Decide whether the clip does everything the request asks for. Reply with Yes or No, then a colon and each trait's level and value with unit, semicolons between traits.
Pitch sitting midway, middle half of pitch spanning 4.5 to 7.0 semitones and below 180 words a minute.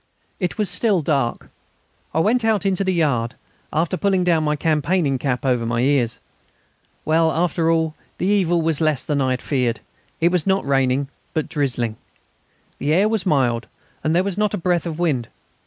No: medium, 160 Hz; average, 5.0 semitones; average, 185 wpm